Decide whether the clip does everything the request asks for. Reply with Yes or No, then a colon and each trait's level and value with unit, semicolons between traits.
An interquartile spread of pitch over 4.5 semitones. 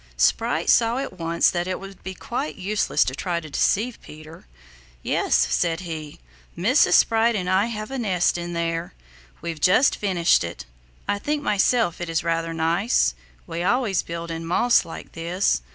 No: average, 4.1 semitones